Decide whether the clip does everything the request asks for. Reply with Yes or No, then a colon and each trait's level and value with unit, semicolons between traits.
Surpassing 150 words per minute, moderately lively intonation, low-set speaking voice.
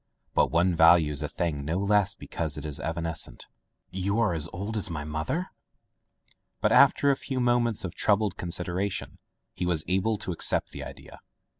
Yes: average, 165 wpm; average, 4.1 semitones; very low, 90 Hz